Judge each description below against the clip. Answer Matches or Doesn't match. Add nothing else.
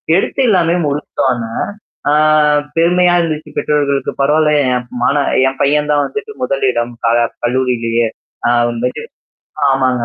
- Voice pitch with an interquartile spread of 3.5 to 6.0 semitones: Matches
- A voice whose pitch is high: Doesn't match